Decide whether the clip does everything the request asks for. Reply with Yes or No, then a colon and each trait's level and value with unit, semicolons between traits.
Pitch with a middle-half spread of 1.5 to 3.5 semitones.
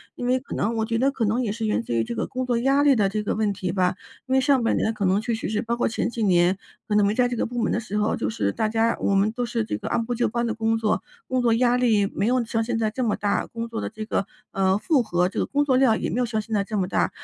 Yes: average, 2.8 semitones